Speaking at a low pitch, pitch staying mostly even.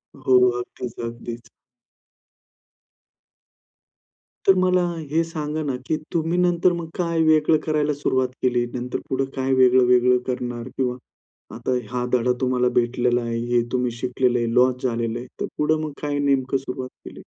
No: low, 130 Hz; average, 3.4 semitones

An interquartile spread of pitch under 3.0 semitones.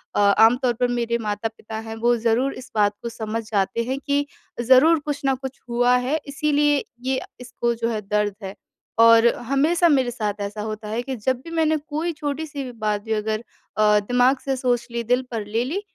No: average, 3.9 semitones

